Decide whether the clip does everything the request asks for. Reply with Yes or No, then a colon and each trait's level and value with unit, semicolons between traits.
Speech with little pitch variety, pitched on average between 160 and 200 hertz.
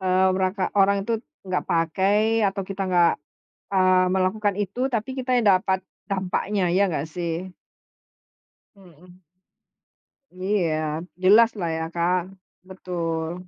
Yes: narrow, 1.8 semitones; medium, 185 Hz